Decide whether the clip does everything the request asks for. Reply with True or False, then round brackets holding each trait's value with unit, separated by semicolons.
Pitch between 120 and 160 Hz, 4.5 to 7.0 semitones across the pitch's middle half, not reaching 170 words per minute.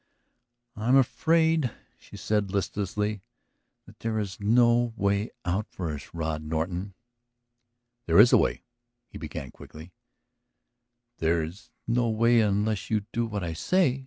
False (105 Hz; 5.1 semitones; 140 wpm)